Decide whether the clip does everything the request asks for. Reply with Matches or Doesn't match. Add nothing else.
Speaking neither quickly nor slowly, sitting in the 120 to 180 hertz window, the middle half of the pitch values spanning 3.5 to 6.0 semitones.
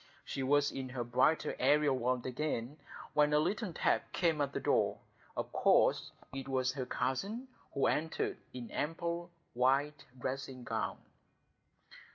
Doesn't match